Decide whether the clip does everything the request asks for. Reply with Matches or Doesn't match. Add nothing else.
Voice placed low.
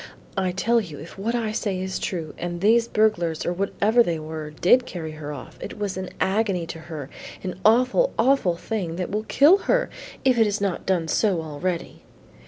Doesn't match